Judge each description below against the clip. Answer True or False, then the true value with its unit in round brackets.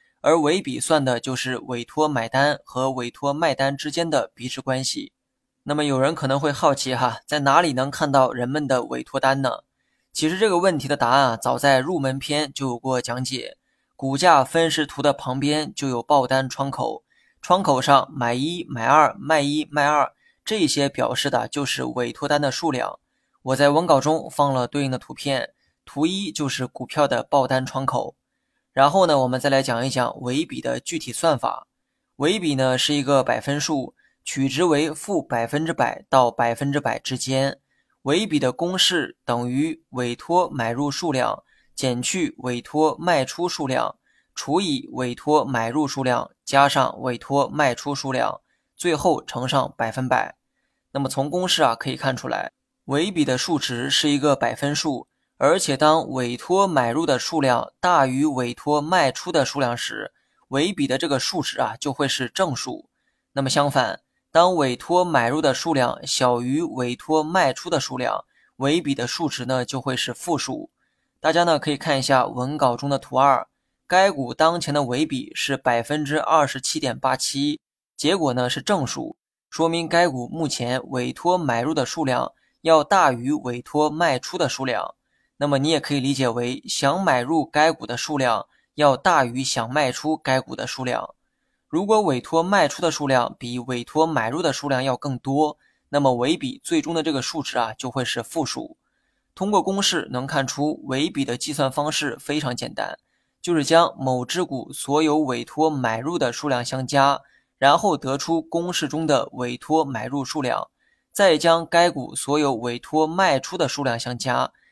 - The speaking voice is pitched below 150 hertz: True (140 Hz)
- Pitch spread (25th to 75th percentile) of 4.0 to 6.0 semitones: False (3.4 semitones)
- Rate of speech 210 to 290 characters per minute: True (255 characters per minute)